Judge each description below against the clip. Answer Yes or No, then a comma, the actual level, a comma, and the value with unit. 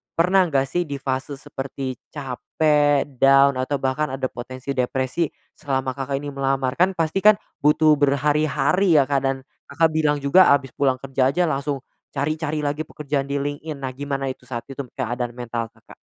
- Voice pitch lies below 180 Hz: Yes, medium, 140 Hz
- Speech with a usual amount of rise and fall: No, narrow, 2.1 semitones